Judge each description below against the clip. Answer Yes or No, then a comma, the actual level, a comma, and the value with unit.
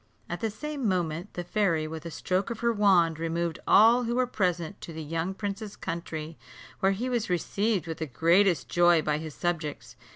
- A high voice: No, medium, 175 Hz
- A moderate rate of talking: Yes, average, 195 wpm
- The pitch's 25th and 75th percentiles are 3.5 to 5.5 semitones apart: Yes, average, 4.2 semitones